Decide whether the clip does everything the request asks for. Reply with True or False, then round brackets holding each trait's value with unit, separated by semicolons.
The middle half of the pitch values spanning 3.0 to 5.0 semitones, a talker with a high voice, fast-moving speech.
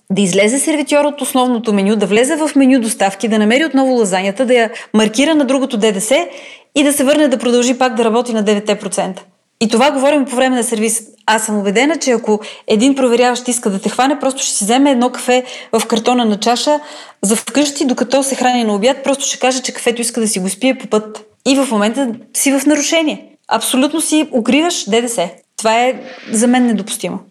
True (3.8 semitones; 245 Hz; 205 wpm)